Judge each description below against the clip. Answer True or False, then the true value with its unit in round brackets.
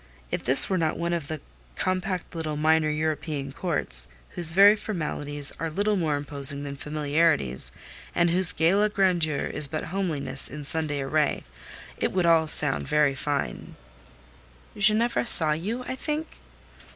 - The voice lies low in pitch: False (160 Hz)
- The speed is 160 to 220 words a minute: False (150 wpm)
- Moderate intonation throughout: True (4.1 semitones)